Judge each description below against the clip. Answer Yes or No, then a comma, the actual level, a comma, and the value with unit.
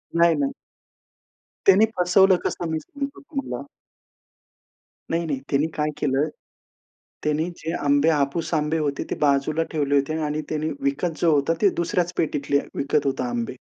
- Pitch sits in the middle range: Yes, medium, 155 Hz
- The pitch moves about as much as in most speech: Yes, average, 3.0 semitones